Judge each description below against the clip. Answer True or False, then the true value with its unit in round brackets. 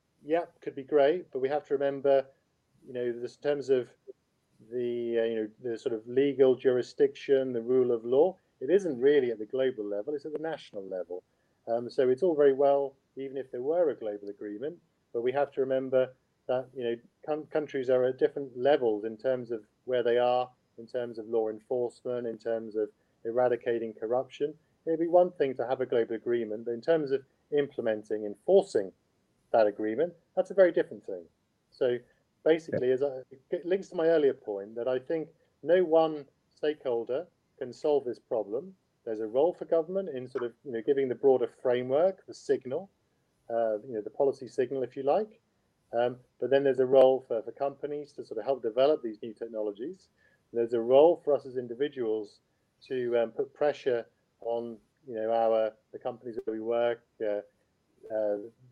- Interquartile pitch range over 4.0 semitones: True (4.5 semitones)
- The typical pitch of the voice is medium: False (130 Hz)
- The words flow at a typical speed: False (195 wpm)